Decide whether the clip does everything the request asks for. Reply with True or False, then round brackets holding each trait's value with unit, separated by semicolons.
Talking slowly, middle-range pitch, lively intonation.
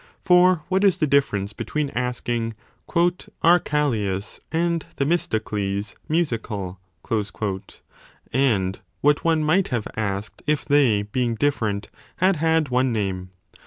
False (120 wpm; 130 Hz; 7.4 semitones)